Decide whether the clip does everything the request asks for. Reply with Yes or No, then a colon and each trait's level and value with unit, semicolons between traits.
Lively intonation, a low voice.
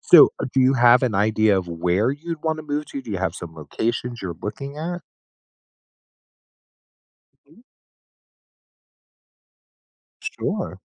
Yes: wide, 6.9 semitones; low, 120 Hz